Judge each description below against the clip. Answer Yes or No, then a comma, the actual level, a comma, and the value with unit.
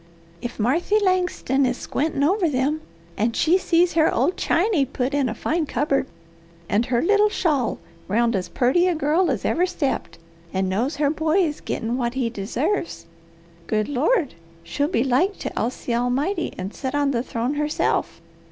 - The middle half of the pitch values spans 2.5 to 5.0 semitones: No, wide, 5.5 semitones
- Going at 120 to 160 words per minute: No, average, 175 wpm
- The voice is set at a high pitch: Yes, very high, 280 Hz